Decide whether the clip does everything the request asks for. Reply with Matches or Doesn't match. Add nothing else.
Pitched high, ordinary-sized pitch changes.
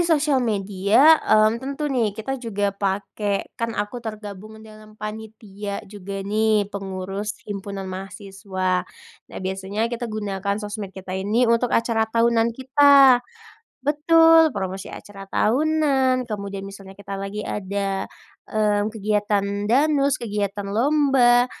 Matches